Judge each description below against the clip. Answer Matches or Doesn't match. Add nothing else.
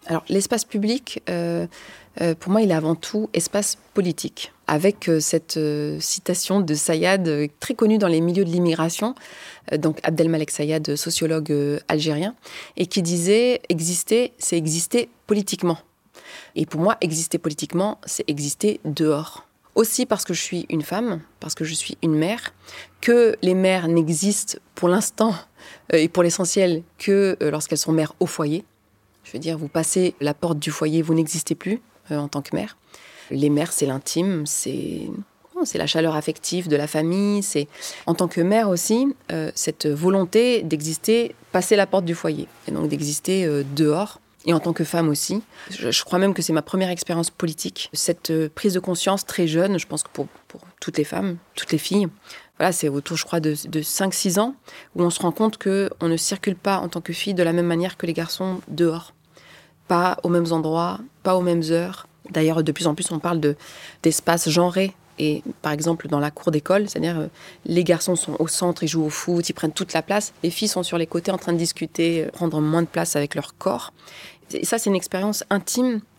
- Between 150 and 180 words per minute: Doesn't match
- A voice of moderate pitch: Matches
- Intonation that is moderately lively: Matches